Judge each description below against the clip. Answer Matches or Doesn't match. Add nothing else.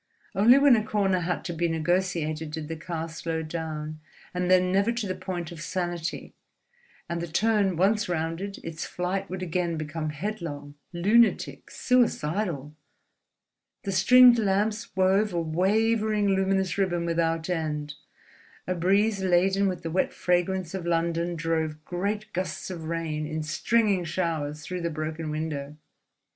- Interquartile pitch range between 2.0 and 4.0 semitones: Matches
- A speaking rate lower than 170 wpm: Matches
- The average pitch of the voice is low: Doesn't match